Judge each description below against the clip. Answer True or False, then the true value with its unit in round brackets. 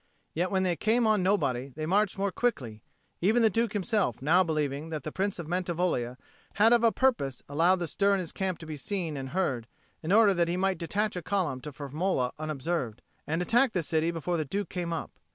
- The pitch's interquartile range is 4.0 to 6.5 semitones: True (4.6 semitones)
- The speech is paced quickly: True (220 wpm)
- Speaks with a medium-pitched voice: True (175 Hz)